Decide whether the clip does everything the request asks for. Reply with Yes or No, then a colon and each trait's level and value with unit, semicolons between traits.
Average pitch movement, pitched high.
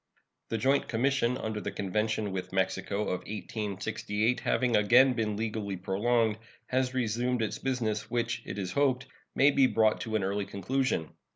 No: average, 3.3 semitones; low, 110 Hz